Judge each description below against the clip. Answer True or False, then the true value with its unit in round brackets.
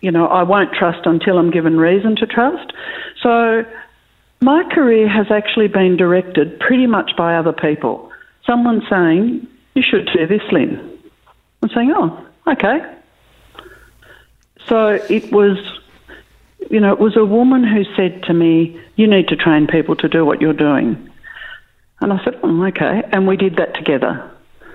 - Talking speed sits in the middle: True (160 wpm)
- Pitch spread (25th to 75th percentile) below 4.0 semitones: False (5.6 semitones)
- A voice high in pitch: True (200 Hz)